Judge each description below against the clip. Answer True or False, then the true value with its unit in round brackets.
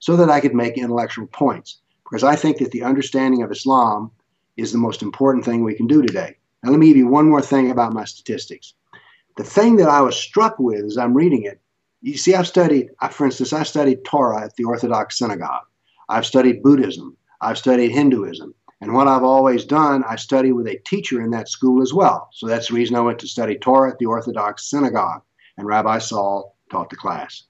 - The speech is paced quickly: True (215 wpm)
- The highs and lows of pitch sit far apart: False (3.7 semitones)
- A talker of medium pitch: False (130 Hz)